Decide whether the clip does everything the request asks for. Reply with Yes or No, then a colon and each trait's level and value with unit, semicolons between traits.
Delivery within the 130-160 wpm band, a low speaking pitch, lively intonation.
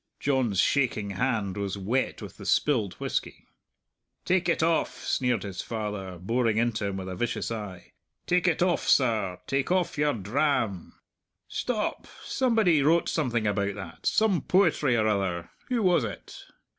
Yes: average, 155 wpm; low, 115 Hz; wide, 7.0 semitones